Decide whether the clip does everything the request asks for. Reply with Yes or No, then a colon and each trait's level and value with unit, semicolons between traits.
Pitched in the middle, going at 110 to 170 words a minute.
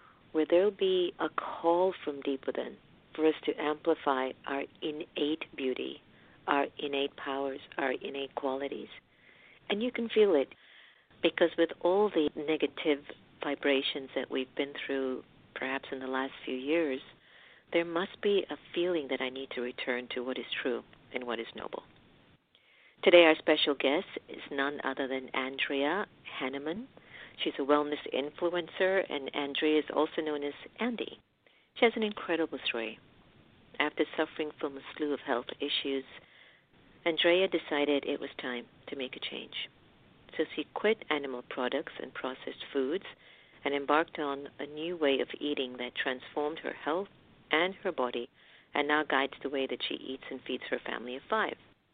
Yes: medium, 145 Hz; average, 165 wpm